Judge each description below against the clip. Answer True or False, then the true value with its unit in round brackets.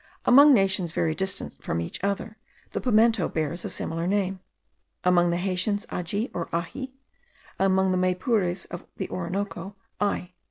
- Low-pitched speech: False (190 Hz)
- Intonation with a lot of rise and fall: False (2.7 semitones)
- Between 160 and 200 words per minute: False (150 wpm)